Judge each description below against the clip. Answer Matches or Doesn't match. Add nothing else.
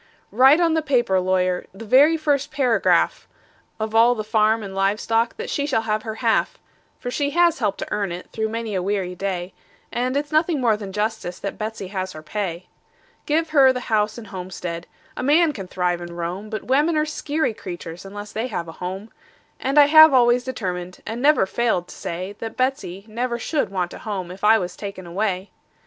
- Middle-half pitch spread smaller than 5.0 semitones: Doesn't match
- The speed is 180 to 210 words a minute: Matches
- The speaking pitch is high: Matches